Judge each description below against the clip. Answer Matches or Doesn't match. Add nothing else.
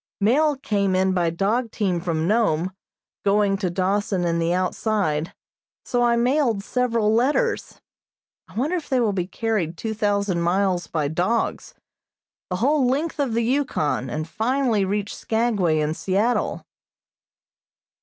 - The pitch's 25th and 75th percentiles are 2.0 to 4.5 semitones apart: Doesn't match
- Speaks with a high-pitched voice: Matches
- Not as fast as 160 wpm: Matches